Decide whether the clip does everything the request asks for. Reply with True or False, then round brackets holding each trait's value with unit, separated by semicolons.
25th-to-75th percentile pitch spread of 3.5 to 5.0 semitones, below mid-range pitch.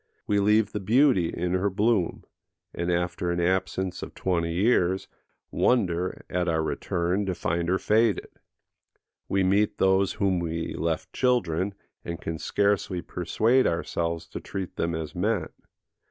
False (2.9 semitones; 95 Hz)